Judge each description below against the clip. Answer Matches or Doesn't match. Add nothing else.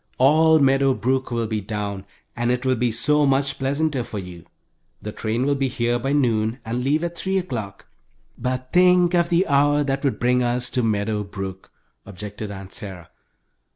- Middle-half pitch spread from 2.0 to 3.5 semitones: Doesn't match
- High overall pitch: Doesn't match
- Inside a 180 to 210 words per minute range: Matches